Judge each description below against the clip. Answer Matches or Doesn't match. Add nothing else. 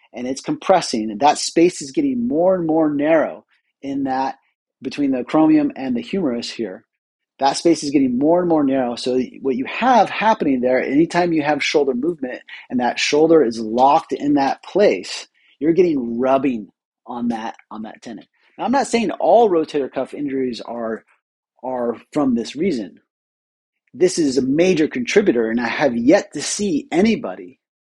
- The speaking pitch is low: Doesn't match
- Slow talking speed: Doesn't match